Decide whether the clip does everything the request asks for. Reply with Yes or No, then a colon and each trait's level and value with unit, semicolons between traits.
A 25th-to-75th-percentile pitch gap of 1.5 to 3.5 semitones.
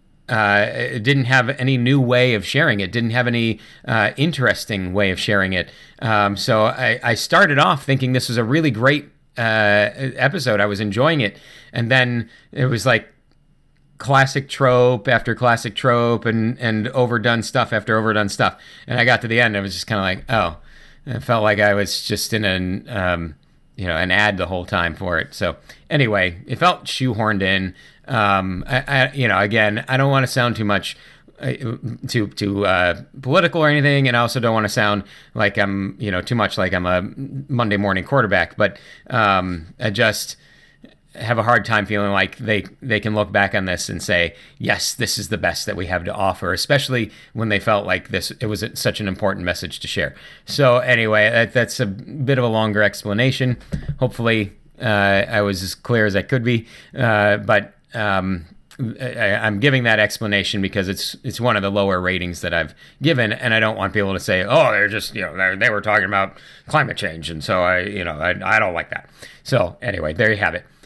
No: average, 4.0 semitones